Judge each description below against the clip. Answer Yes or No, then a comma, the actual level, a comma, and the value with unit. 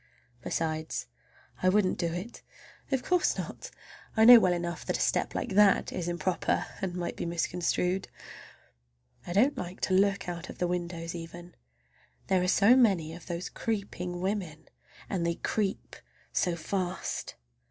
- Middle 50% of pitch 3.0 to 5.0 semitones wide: No, narrow, 2.5 semitones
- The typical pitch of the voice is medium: Yes, medium, 180 Hz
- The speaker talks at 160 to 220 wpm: No, average, 150 wpm